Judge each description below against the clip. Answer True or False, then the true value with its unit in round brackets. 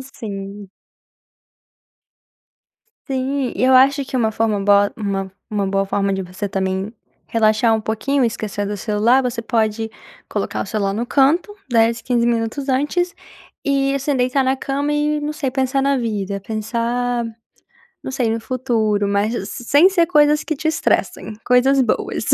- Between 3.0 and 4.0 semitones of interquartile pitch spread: False (4.4 semitones)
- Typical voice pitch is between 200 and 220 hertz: False (235 Hz)